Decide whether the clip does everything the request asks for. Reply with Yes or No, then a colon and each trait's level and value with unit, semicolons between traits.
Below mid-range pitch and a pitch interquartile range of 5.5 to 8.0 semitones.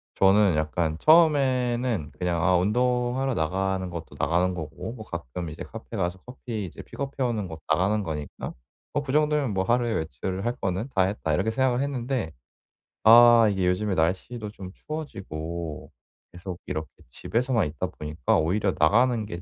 Yes: low, 100 Hz; wide, 6.2 semitones